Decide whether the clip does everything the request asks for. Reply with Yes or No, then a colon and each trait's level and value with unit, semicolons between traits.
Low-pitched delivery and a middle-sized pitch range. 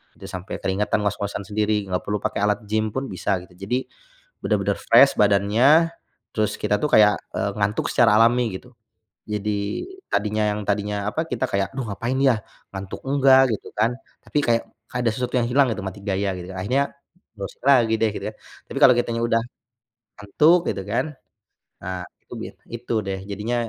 Yes: low, 105 Hz; average, 3.2 semitones